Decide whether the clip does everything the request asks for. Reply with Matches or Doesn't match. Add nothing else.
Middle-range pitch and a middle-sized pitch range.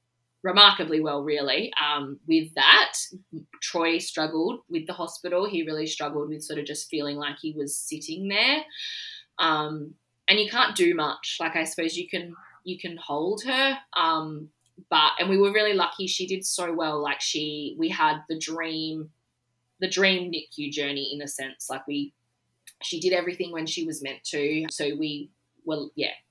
Matches